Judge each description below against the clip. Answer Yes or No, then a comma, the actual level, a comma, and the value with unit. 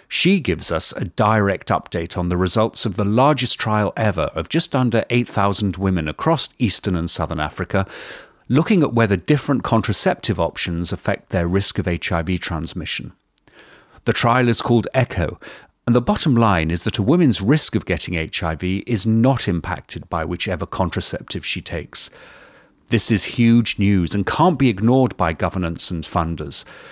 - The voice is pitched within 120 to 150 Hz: No, low, 100 Hz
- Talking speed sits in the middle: Yes, average, 165 wpm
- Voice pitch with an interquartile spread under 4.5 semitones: No, average, 5.0 semitones